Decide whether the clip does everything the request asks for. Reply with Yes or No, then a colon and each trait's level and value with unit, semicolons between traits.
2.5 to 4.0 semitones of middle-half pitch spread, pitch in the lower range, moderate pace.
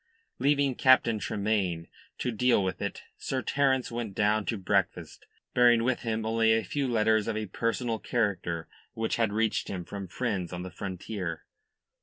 Yes: average, 3.4 semitones; low, 110 Hz; average, 165 wpm